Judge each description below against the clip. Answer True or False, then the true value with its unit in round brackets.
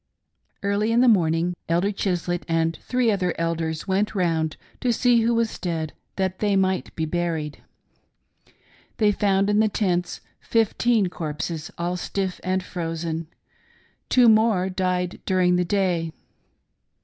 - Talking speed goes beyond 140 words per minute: False (135 wpm)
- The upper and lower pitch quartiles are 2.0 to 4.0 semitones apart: True (3.7 semitones)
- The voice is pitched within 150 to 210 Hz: True (185 Hz)